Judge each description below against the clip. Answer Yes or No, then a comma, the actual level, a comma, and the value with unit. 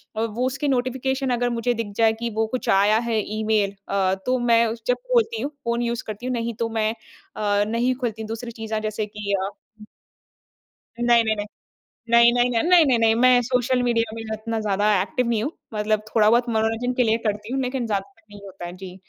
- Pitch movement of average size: No, narrow, 2.3 semitones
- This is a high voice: Yes, high, 230 Hz